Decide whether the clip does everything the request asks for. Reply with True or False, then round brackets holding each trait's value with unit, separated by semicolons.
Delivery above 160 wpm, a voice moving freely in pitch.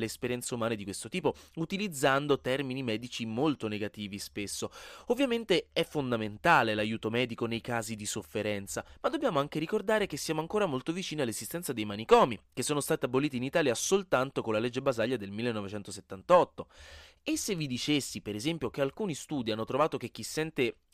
True (170 wpm; 6.1 semitones)